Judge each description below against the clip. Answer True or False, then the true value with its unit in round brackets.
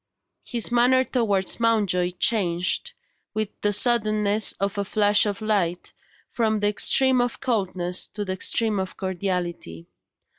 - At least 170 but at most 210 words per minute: False (135 wpm)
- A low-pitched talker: False (205 Hz)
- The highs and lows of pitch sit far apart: False (3.3 semitones)